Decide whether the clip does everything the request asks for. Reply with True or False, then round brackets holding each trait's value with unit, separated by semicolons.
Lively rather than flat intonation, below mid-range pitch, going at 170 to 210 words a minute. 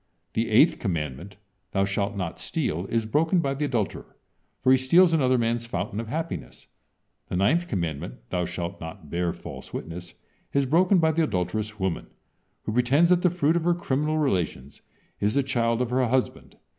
True (8.1 semitones; 115 Hz; 180 wpm)